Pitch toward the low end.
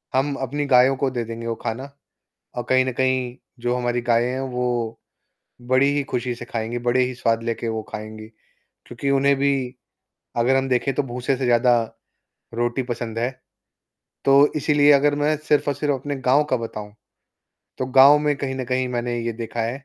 Yes: low, 125 Hz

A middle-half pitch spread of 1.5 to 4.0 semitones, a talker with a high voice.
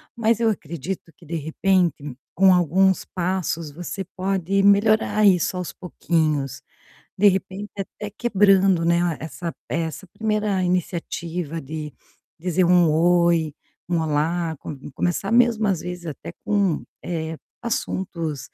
No: average, 3.0 semitones; medium, 175 Hz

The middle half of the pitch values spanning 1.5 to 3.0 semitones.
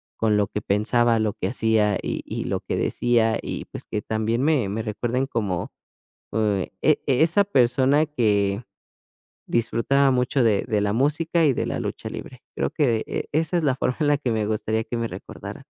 No: average, 4.4 semitones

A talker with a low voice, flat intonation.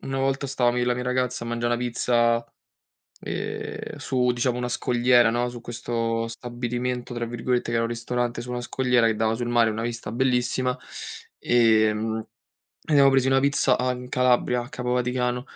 Yes: low, 120 Hz; narrow, 1.1 semitones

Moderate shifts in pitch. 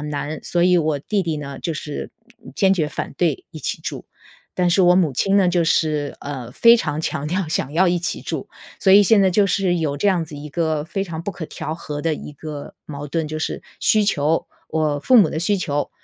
Yes: average, 3.7 semitones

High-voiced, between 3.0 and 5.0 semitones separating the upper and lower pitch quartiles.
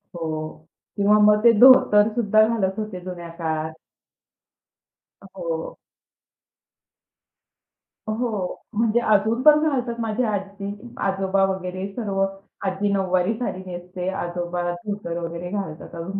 Yes: high, 195 Hz; average, 3.3 semitones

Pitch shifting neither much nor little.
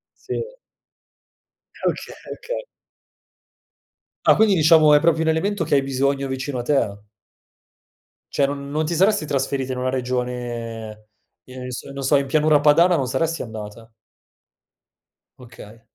Yes: average, 4.0 semitones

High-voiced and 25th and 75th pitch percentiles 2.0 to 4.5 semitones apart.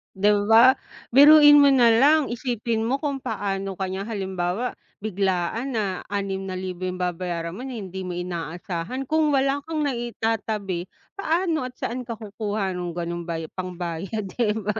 No: high, 205 Hz; wide, 5.4 semitones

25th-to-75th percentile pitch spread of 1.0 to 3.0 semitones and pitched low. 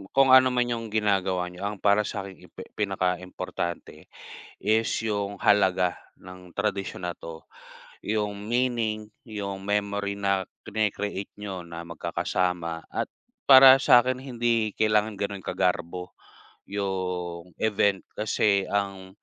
Yes: average, 2.7 semitones; low, 100 Hz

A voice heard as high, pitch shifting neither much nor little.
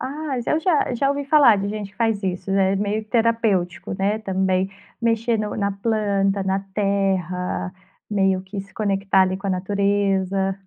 No: high, 200 Hz; narrow, 2.3 semitones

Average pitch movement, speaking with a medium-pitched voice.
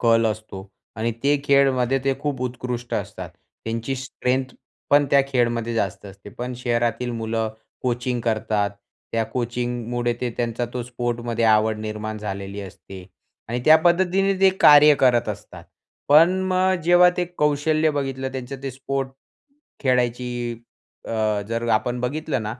No: average, 3.2 semitones; low, 125 Hz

